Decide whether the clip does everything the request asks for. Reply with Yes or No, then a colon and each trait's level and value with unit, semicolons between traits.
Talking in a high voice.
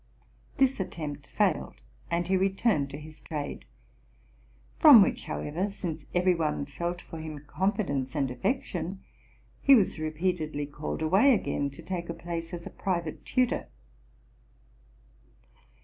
No: medium, 170 Hz